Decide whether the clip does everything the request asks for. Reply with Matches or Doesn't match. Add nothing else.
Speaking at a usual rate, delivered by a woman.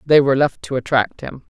Doesn't match